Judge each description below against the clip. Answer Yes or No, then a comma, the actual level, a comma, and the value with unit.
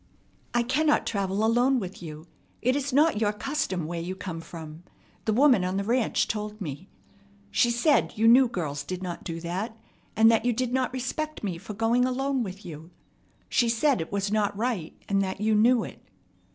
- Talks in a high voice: Yes, high, 215 Hz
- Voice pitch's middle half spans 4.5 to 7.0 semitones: Yes, average, 5.1 semitones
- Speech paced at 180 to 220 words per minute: Yes, average, 195 wpm